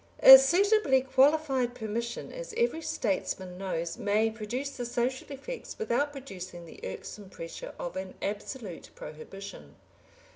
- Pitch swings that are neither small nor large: No, wide, 6.4 semitones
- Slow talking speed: Yes, slow, 125 wpm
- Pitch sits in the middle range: No, high, 235 Hz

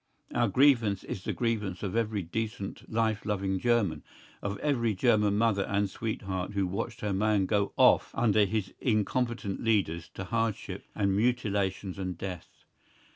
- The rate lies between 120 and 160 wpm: Yes, average, 150 wpm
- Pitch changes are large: No, average, 2.7 semitones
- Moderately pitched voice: No, low, 105 Hz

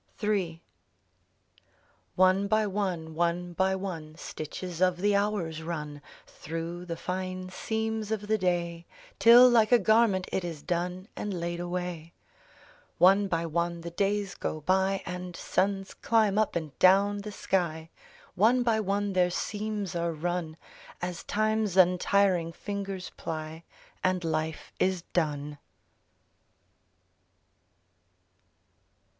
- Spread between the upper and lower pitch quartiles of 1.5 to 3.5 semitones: Yes, average, 3.1 semitones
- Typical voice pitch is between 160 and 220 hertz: Yes, medium, 185 Hz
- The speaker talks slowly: Yes, slow, 130 wpm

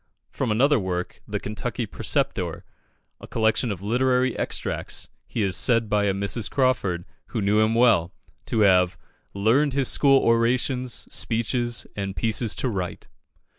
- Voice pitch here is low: Yes, low, 115 Hz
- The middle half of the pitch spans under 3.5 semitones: No, average, 3.9 semitones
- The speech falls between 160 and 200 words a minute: No, average, 145 wpm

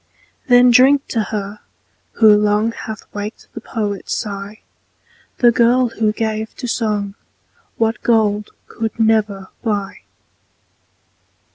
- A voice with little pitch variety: Yes, narrow, 1.8 semitones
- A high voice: Yes, high, 220 Hz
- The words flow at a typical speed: No, slow, 115 wpm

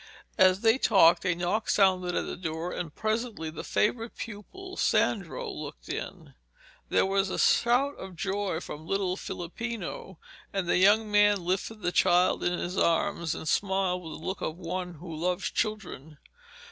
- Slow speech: No, average, 165 wpm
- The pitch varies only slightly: No, average, 3.2 semitones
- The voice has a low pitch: No, medium, 185 Hz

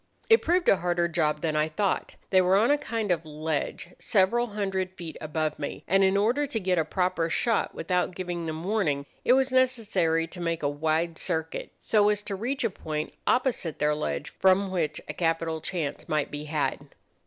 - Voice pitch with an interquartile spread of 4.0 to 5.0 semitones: Yes, average, 4.6 semitones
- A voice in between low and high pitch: Yes, medium, 175 Hz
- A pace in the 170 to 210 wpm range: Yes, average, 200 wpm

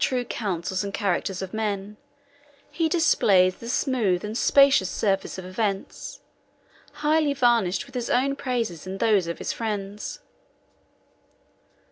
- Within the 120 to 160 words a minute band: Yes, average, 150 wpm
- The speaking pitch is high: Yes, high, 210 Hz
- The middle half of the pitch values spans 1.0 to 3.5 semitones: No, average, 4.7 semitones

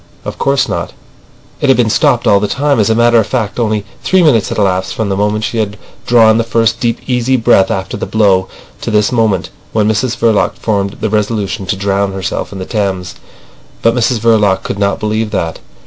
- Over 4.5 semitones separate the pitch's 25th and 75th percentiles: No, average, 2.7 semitones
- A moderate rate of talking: No, fast, 210 wpm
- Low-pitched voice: Yes, low, 110 Hz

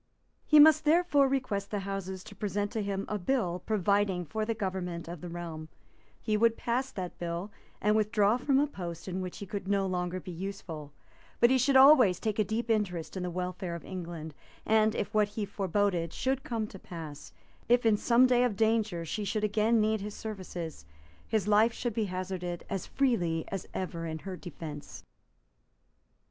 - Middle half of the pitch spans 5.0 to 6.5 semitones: No, average, 3.8 semitones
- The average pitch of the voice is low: No, high, 200 Hz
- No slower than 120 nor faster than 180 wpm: No, average, 190 wpm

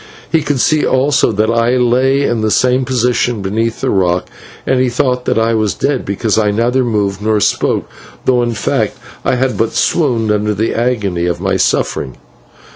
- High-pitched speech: No, low, 115 Hz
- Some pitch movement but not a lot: Yes, average, 3.3 semitones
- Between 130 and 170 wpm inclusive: No, average, 190 wpm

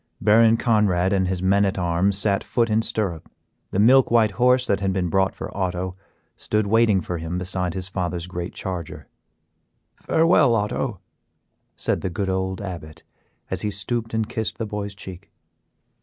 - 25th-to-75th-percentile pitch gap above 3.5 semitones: No, average, 3.1 semitones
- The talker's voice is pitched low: Yes, very low, 95 Hz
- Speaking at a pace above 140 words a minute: Yes, average, 170 wpm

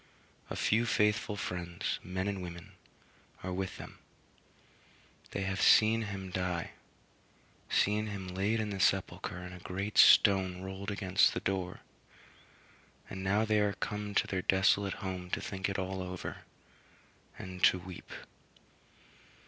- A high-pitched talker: No, very low, 95 Hz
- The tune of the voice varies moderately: No, narrow, 1.8 semitones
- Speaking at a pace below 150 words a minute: Yes, average, 140 wpm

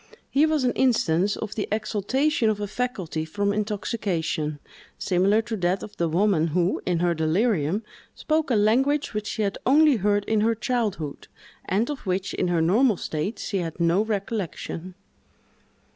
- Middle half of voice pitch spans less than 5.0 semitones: Yes, average, 4.4 semitones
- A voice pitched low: No, high, 205 Hz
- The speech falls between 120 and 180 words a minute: Yes, average, 165 wpm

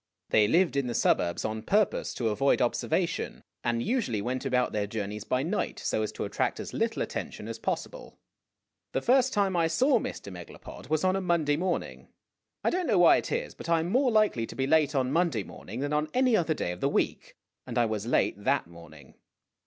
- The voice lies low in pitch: No, medium, 145 Hz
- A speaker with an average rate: No, fast, 215 wpm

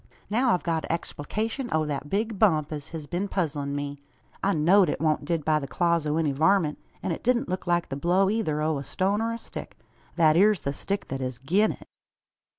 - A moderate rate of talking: No, fast, 225 wpm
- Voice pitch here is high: No, medium, 165 Hz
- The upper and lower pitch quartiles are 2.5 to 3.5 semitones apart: No, average, 4.9 semitones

